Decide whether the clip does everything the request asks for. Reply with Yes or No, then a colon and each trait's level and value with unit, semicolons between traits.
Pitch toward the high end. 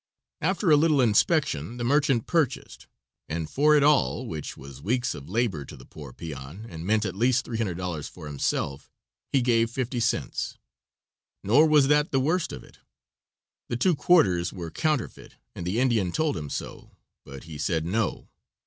No: low, 115 Hz